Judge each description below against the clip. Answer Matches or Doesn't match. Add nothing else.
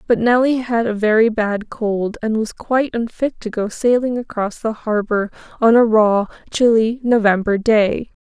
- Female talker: Matches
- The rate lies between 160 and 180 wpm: Matches